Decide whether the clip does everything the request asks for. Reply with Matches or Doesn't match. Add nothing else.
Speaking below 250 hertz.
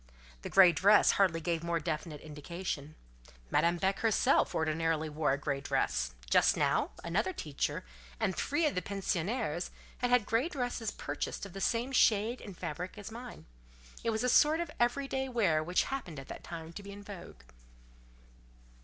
Matches